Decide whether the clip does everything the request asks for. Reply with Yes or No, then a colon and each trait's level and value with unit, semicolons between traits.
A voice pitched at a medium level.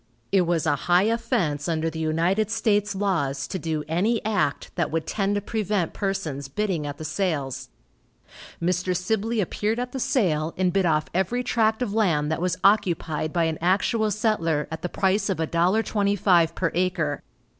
Yes: medium, 180 Hz